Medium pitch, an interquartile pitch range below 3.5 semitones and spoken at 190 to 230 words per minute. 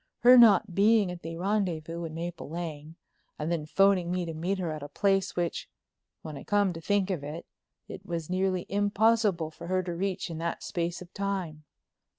Yes: medium, 175 Hz; average, 3.1 semitones; average, 195 wpm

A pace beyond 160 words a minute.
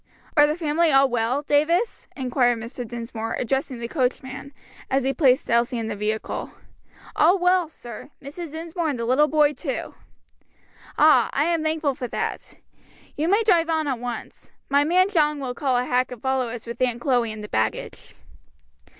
Yes: average, 180 wpm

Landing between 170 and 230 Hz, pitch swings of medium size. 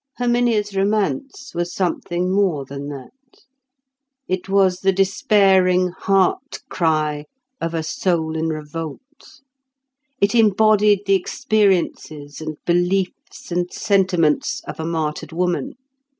Yes: medium, 185 Hz; average, 3.9 semitones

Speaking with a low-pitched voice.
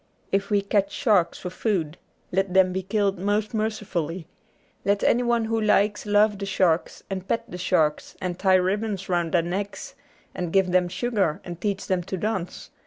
No: high, 195 Hz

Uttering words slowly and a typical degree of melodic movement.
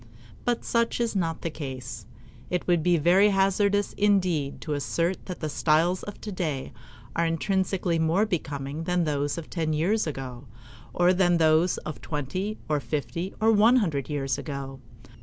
No: average, 160 wpm; average, 4.4 semitones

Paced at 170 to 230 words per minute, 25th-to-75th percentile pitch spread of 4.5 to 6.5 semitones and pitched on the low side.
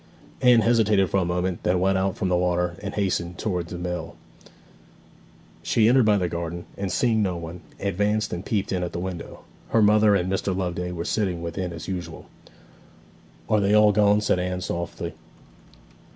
No: average, 180 wpm; average, 2.8 semitones; very low, 95 Hz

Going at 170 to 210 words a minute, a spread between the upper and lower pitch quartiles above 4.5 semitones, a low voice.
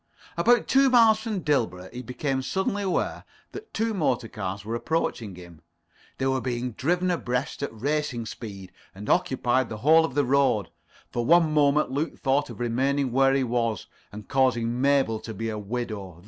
Yes: average, 175 wpm; average, 5.1 semitones; low, 130 Hz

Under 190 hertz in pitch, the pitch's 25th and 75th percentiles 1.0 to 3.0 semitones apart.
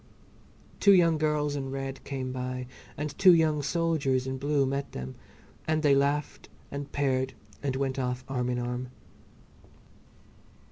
Yes: medium, 140 Hz; narrow, 2.4 semitones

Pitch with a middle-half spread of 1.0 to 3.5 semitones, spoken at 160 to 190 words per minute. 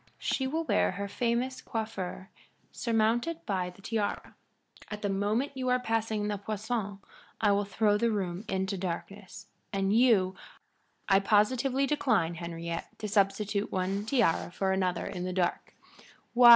No: average, 3.2 semitones; average, 150 wpm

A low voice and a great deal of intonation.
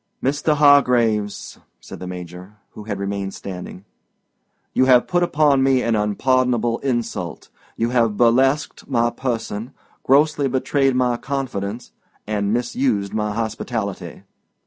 No: low, 120 Hz; average, 4.2 semitones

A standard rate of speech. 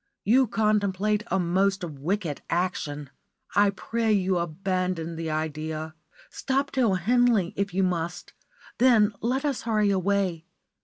No: slow, 125 wpm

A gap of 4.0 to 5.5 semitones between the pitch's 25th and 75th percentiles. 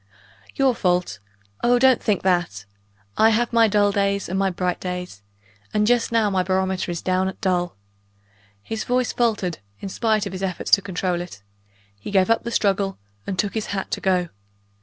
No: average, 3.3 semitones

